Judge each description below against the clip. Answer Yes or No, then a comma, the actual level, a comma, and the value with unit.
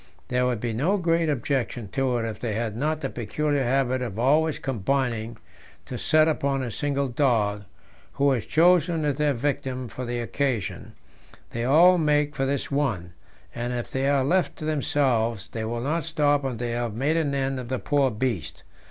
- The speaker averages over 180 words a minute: Yes, average, 190 wpm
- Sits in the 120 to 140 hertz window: Yes, low, 135 Hz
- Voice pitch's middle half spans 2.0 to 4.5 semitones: Yes, average, 3.7 semitones